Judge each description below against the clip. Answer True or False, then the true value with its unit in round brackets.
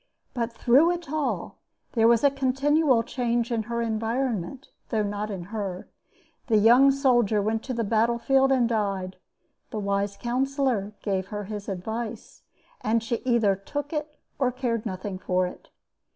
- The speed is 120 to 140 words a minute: False (160 wpm)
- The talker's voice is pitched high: True (230 Hz)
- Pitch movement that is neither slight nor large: True (4.0 semitones)